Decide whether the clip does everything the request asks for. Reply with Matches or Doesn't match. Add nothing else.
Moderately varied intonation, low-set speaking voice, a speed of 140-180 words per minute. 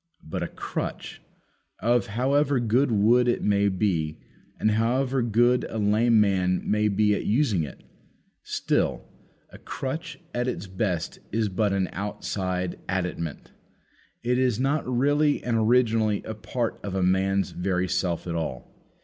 Matches